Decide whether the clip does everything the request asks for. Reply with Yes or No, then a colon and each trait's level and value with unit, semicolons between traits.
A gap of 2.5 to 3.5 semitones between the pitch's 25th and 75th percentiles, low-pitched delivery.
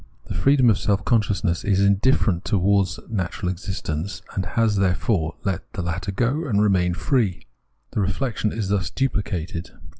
Yes: average, 3.2 semitones; low, 100 Hz